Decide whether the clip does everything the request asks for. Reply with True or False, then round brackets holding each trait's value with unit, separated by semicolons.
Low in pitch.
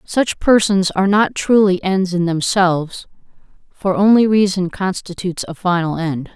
False (190 Hz)